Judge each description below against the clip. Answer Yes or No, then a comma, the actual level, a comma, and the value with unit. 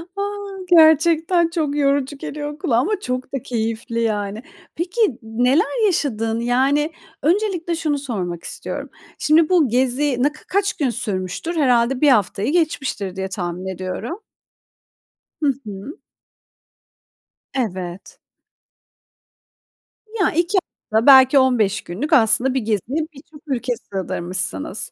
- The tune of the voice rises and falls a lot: Yes, wide, 5.9 semitones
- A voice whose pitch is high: Yes, very high, 265 Hz